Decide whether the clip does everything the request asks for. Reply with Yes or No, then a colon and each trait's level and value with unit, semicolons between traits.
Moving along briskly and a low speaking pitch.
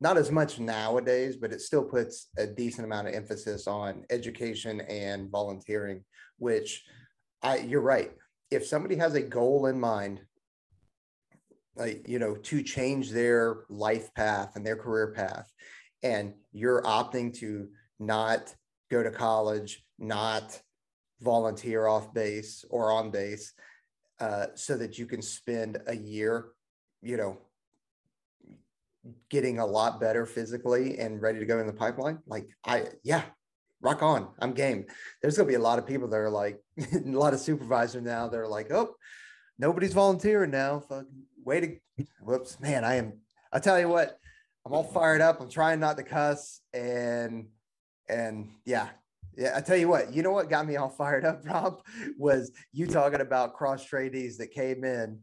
No: average, 165 wpm; low, 120 Hz